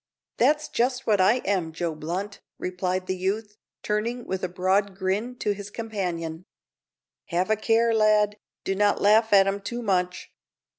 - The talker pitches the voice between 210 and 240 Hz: No, high, 200 Hz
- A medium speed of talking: Yes, average, 160 wpm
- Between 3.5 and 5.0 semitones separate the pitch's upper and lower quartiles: No, average, 2.9 semitones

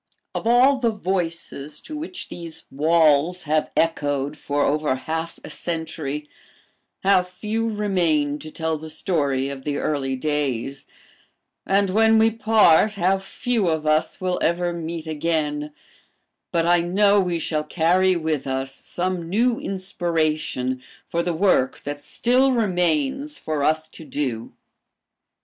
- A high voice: No, medium, 165 Hz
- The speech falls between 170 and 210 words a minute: No, average, 140 wpm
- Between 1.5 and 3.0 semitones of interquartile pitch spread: No, average, 4.4 semitones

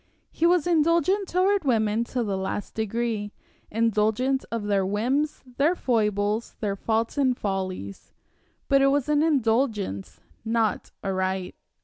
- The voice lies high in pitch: Yes, high, 230 Hz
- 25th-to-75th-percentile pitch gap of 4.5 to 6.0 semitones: Yes, average, 5.2 semitones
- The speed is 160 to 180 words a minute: No, slow, 135 wpm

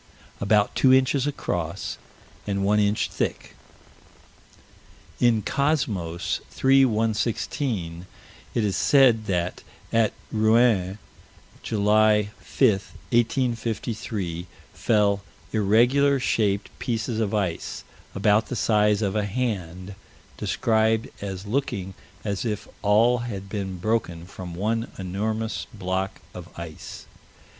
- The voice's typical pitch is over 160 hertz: No, low, 105 Hz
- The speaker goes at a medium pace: No, slow, 105 wpm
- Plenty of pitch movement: No, average, 3.0 semitones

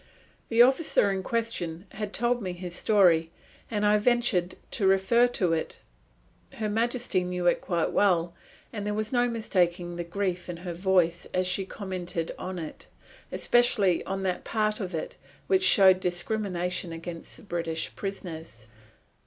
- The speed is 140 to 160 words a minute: Yes, average, 155 wpm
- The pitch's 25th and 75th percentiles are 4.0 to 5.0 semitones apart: No, average, 3.5 semitones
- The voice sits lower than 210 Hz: Yes, high, 190 Hz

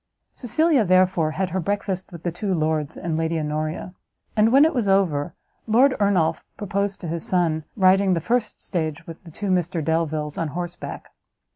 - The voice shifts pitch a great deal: No, average, 3.7 semitones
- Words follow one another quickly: No, average, 175 wpm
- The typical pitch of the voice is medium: Yes, medium, 180 Hz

